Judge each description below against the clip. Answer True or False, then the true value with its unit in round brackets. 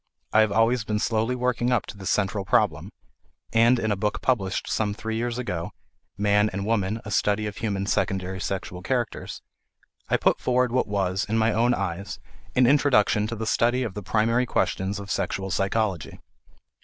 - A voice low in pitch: True (105 Hz)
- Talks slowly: False (180 wpm)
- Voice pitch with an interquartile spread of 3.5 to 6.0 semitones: False (2.9 semitones)